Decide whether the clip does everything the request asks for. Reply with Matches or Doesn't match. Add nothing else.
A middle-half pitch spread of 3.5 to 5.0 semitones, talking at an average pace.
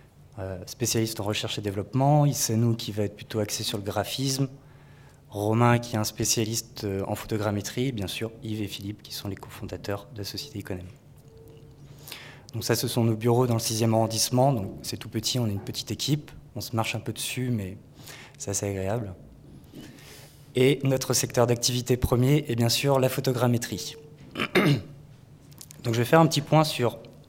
Matches